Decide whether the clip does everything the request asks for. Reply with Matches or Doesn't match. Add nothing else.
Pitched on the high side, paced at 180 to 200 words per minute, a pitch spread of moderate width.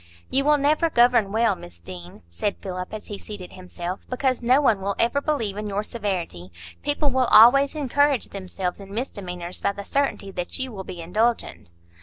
Doesn't match